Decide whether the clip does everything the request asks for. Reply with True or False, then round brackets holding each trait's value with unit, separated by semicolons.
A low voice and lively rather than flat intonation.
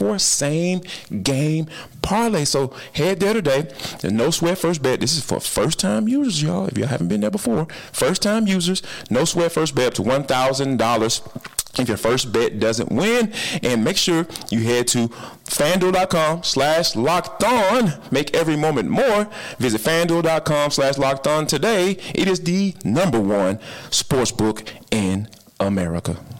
False (155 Hz; 7.0 semitones)